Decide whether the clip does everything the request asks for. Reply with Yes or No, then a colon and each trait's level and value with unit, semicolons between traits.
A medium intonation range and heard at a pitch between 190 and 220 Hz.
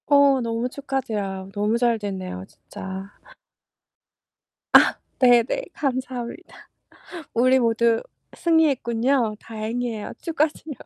No: average, 3.7 semitones; high, 235 Hz